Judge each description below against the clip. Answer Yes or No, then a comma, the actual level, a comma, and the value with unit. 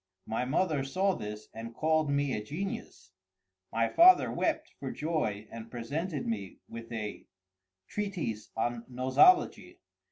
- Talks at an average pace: No, slow, 125 wpm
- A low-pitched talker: Yes, low, 120 Hz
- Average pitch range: No, wide, 6.4 semitones